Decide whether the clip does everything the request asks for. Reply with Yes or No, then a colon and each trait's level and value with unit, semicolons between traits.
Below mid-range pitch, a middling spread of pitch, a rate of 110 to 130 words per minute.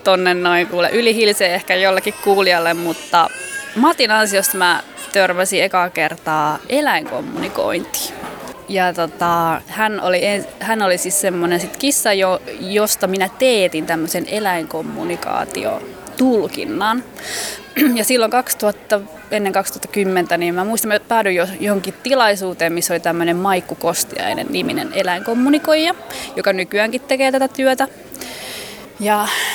No: high, 195 Hz; average, 4.2 semitones; average, 115 wpm